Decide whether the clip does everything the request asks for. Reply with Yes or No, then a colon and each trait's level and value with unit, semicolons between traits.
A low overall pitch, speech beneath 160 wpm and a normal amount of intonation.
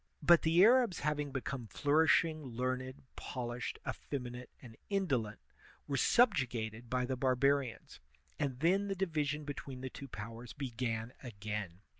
Yes: low, 130 Hz; slow, 135 wpm; average, 4.0 semitones